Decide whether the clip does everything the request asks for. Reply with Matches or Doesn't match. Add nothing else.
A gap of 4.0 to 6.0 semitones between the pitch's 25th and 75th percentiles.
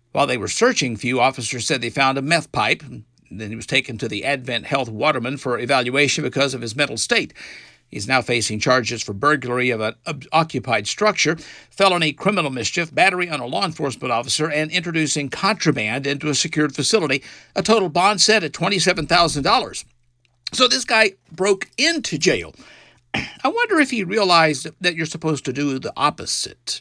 Matches